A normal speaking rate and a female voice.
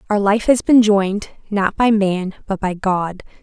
Yes: average, 190 wpm; female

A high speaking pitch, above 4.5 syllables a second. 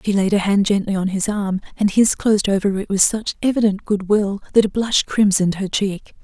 Yes: high, 200 Hz; 5.4 syllables/s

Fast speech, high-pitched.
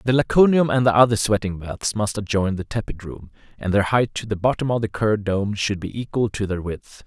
No: fast, 230 wpm; low, 105 Hz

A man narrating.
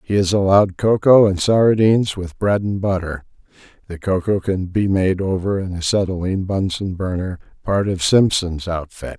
Yes: male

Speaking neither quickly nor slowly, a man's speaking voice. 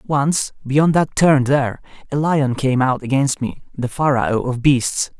Yes: average, 175 wpm; male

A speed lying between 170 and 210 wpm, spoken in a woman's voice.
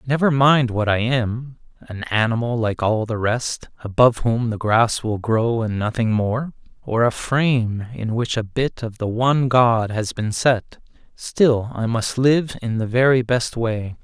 No: average, 175 wpm; male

